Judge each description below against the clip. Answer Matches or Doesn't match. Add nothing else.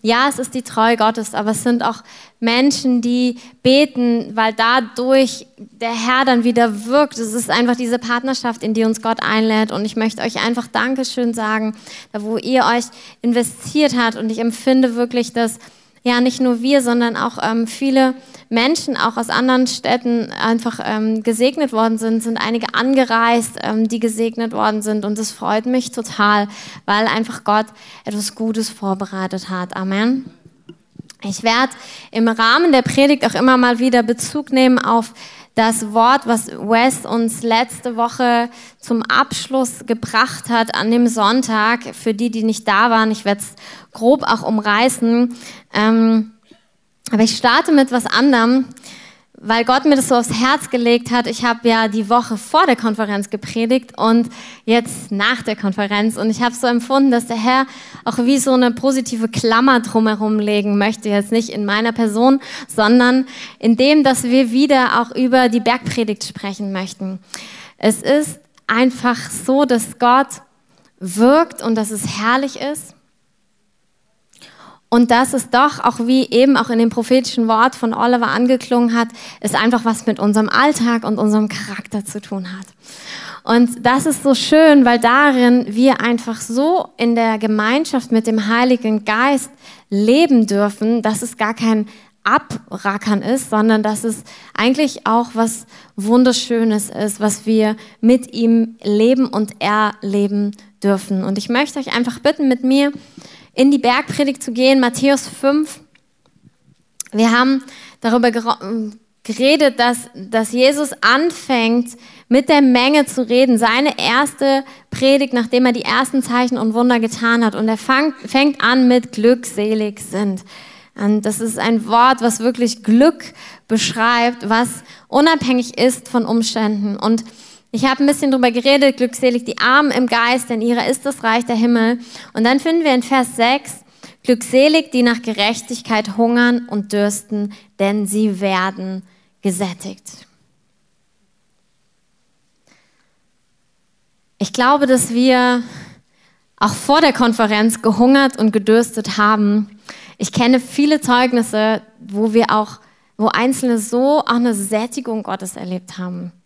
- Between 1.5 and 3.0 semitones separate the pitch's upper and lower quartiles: Matches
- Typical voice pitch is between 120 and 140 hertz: Doesn't match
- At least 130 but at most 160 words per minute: Matches